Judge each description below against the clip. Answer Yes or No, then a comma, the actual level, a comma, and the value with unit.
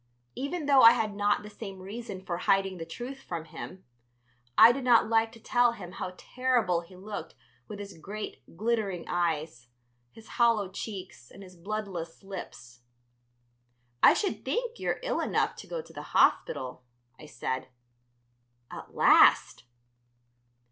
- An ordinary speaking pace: Yes, average, 150 wpm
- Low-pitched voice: No, high, 200 Hz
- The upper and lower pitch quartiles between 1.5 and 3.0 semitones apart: No, average, 4.8 semitones